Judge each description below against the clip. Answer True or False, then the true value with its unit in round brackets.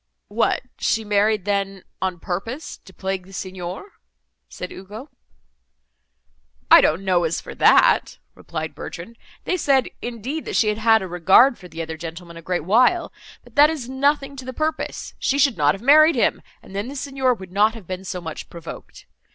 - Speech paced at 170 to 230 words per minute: True (185 wpm)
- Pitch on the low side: False (205 Hz)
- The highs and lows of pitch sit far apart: True (6.3 semitones)